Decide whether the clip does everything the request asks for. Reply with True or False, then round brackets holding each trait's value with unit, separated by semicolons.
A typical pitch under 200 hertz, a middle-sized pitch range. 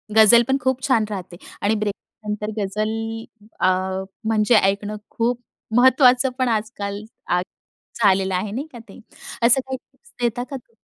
False (220 Hz; 3.4 semitones)